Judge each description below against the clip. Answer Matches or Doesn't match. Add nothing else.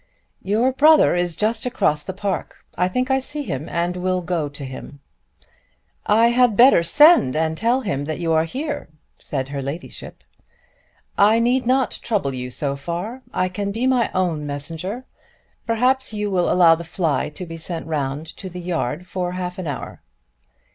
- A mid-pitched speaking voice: Matches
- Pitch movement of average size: Doesn't match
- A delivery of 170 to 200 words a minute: Matches